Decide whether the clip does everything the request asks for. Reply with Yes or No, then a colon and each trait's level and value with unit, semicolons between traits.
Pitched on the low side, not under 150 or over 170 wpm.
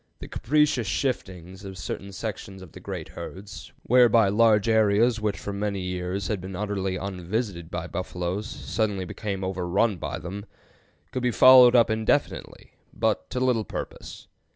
Yes: low, 100 Hz; average, 155 wpm